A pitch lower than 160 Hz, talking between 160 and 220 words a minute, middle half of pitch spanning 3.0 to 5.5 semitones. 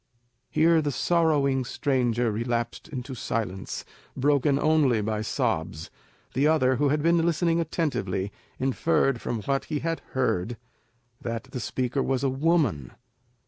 No: low, 135 Hz; slow, 135 wpm; average, 4.6 semitones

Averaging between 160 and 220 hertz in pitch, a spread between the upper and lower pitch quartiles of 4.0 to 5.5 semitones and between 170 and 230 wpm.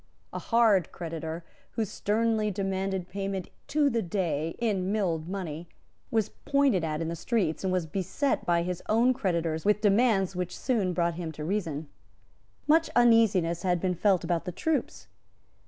No: high, 190 Hz; average, 4.3 semitones; average, 160 wpm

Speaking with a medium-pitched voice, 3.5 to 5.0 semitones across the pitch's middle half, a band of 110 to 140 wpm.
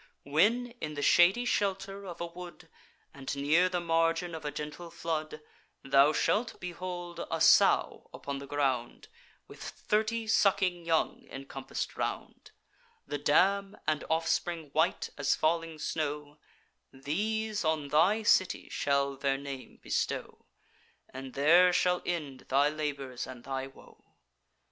Yes: medium, 160 Hz; average, 4.1 semitones; slow, 135 wpm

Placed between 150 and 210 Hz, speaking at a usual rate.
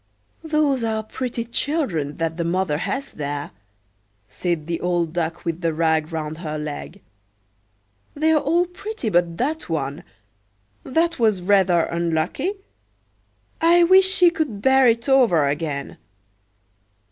No: medium, 185 Hz; slow, 130 wpm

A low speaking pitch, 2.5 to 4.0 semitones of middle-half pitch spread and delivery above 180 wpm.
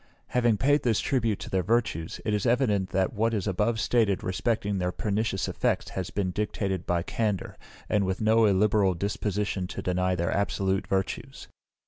No: low, 100 Hz; average, 2.8 semitones; average, 170 wpm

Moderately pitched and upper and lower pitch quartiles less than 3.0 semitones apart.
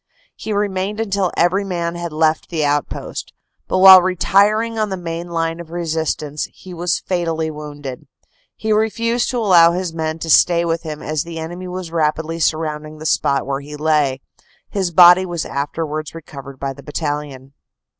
No: medium, 165 Hz; average, 3.3 semitones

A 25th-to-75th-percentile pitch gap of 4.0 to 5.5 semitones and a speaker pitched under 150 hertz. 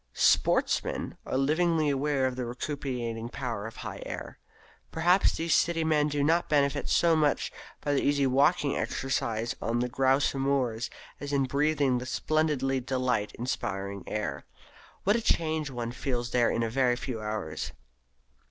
No: average, 3.6 semitones; low, 135 Hz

